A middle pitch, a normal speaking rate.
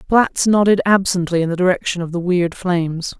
Yes: medium, 180 Hz; average, 190 wpm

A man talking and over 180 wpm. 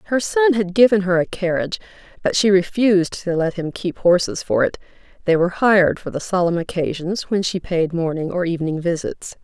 No: female; average, 195 wpm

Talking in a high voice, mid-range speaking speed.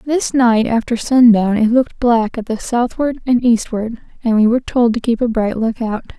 No: high, 235 Hz; fast, 215 wpm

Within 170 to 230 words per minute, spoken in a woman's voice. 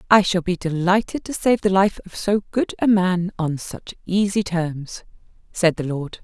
Yes: average, 195 wpm; female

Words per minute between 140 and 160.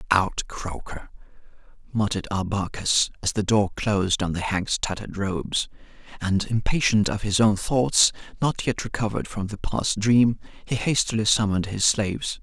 Yes: average, 150 wpm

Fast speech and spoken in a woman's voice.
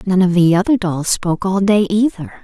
Yes: fast, 220 wpm; female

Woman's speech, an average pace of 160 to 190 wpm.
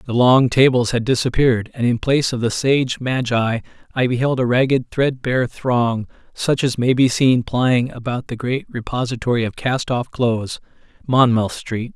No: male; average, 170 wpm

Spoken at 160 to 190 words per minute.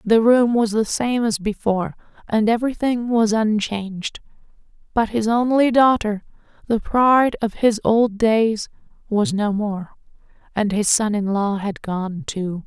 No: average, 150 wpm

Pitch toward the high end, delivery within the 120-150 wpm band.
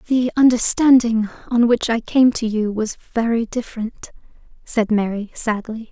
Yes: high, 230 Hz; average, 140 wpm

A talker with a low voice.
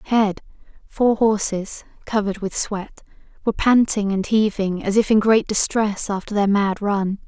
No: high, 205 Hz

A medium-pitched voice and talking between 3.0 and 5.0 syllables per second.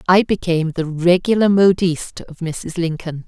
Yes: medium, 175 Hz; 4.9 syllables/s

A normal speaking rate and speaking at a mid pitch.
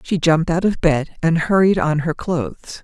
No: fast, 210 wpm; medium, 170 Hz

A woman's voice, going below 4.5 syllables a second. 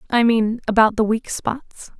Yes: female; 4.2 syllables/s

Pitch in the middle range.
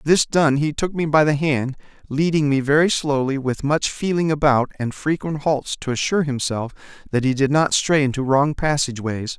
Yes: medium, 145 Hz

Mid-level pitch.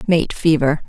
Yes: medium, 155 Hz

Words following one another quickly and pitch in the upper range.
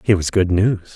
No: fast, 250 wpm; very low, 95 Hz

